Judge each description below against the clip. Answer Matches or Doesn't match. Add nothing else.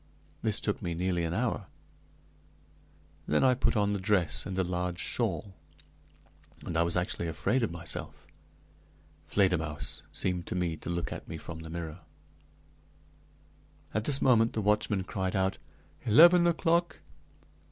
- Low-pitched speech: Matches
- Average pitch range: Matches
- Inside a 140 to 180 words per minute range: Matches